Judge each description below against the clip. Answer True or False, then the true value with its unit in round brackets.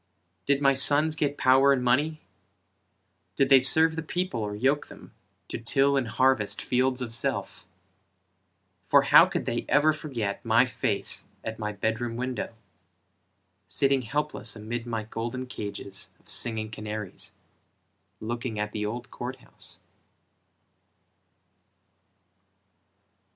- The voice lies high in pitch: False (125 Hz)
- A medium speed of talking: False (130 wpm)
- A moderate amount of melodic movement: True (3.8 semitones)